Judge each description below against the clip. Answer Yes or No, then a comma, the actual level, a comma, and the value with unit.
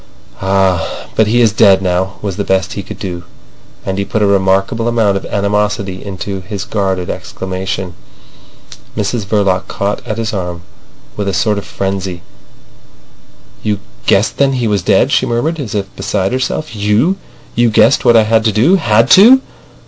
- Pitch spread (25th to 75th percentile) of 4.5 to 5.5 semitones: No, average, 2.7 semitones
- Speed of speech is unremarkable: Yes, average, 170 wpm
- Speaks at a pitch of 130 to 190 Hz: No, low, 100 Hz